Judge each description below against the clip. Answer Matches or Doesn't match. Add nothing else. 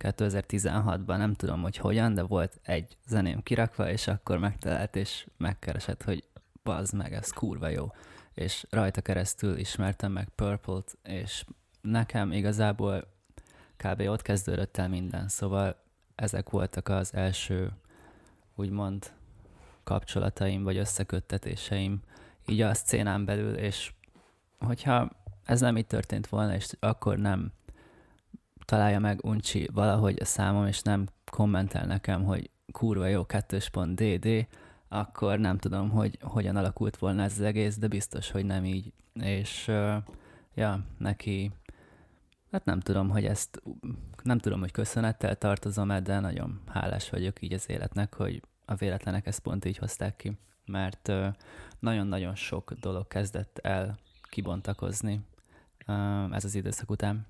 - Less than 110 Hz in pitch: Matches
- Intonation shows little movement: Matches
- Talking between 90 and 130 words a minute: Doesn't match